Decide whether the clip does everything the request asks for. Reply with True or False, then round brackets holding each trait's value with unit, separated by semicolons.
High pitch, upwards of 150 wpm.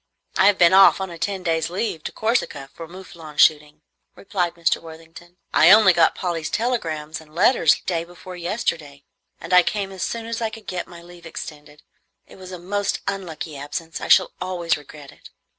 False (175 Hz; 195 wpm)